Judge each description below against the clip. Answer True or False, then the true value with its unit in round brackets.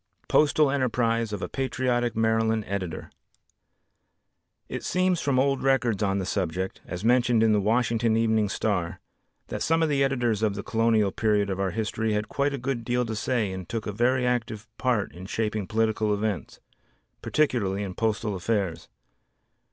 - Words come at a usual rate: True (165 wpm)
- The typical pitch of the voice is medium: False (110 Hz)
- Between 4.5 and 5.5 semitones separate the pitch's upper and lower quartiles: False (3.2 semitones)